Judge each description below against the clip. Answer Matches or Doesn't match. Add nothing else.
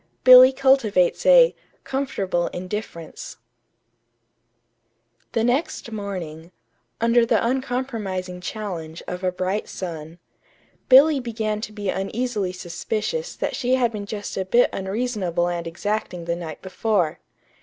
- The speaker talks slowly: Matches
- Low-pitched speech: Doesn't match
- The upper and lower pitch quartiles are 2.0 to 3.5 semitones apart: Doesn't match